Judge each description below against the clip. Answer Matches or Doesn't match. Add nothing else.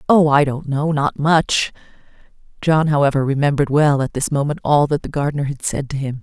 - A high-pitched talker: Doesn't match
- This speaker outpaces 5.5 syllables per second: Matches